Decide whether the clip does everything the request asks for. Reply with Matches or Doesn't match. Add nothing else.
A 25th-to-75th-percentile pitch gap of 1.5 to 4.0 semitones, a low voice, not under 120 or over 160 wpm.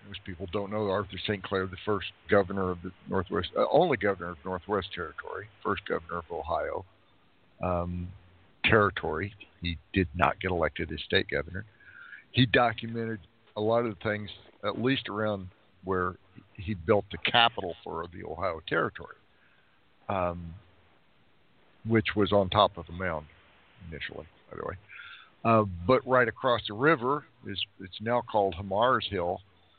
Matches